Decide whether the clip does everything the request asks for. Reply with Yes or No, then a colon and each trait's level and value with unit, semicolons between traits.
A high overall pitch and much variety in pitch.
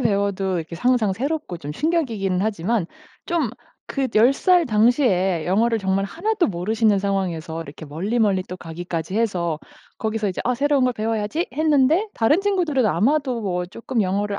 Yes: high, 215 Hz; wide, 6.0 semitones